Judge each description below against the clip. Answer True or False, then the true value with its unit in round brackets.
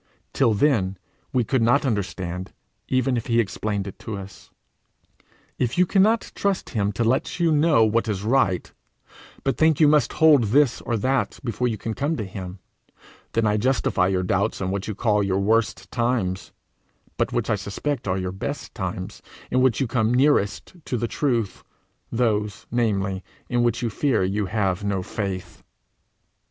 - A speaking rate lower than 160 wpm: False (170 wpm)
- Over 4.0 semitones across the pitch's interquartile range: True (4.7 semitones)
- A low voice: True (110 Hz)